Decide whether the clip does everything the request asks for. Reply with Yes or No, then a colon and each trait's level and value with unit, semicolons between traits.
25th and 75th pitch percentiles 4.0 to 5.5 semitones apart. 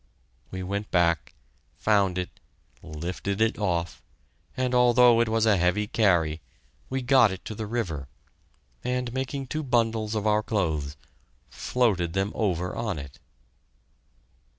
Yes: average, 4.8 semitones